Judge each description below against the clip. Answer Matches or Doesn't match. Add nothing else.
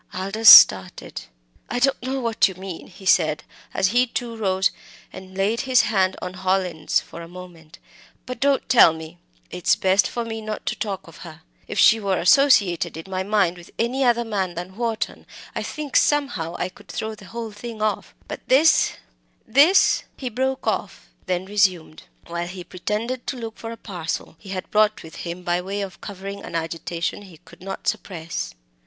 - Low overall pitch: Doesn't match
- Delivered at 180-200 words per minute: Matches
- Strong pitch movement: Doesn't match